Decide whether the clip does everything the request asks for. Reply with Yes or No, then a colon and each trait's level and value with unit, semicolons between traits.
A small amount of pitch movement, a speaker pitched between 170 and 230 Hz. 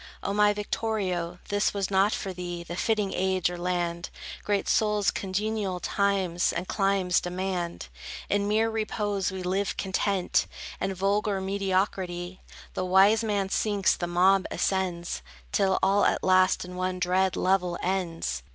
Yes: narrow, 1.9 semitones; high, 190 Hz